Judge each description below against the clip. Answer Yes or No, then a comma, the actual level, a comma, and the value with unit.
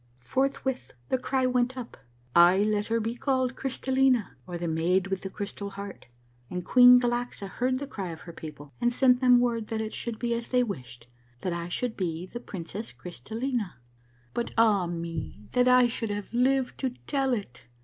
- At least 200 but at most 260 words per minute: Yes, fast, 205 wpm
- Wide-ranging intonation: Yes, wide, 5.9 semitones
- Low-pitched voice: No, high, 225 Hz